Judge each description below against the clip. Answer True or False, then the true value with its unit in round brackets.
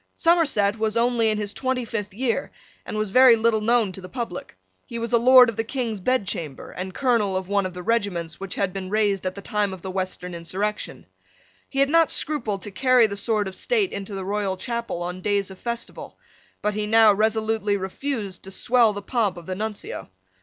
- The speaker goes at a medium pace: False (210 wpm)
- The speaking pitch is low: False (210 Hz)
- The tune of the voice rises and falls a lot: False (3.4 semitones)